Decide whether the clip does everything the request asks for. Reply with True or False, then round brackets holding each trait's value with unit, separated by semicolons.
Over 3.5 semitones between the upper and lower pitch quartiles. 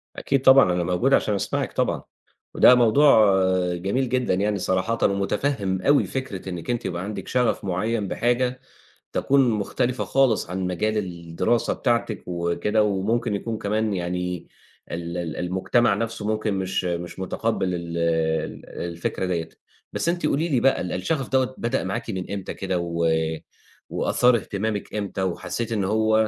True (4.7 semitones)